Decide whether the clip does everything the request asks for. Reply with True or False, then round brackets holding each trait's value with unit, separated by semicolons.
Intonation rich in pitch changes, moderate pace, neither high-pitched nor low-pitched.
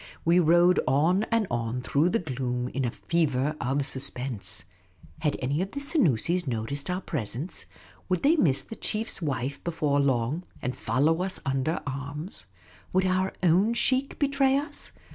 True (6.0 semitones; 160 wpm; 150 Hz)